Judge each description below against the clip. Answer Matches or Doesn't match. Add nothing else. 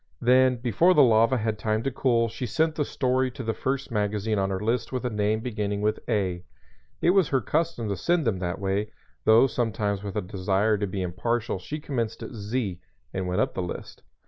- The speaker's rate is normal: Doesn't match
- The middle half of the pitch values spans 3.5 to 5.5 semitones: Matches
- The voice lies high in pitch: Doesn't match